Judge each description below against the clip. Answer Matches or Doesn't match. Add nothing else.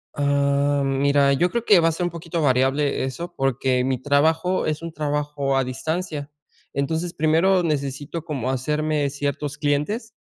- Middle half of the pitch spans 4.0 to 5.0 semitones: Doesn't match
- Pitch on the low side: Doesn't match